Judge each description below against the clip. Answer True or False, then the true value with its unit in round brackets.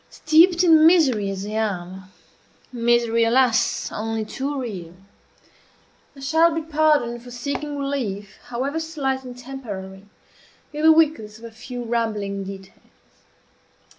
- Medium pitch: False (240 Hz)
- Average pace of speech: False (130 wpm)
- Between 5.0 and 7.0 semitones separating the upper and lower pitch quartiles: True (5.5 semitones)